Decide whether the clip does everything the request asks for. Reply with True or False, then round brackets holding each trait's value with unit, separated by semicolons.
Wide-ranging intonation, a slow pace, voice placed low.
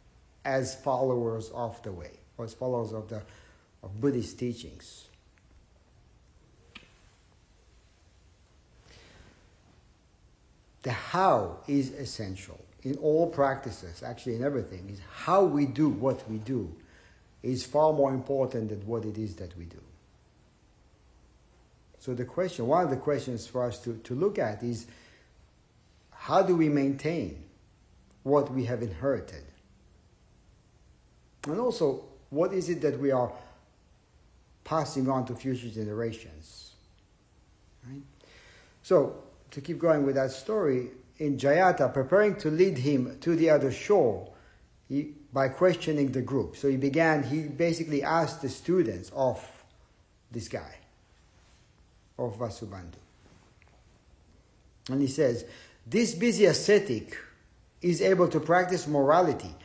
True (6.1 semitones; 125 wpm; 125 Hz)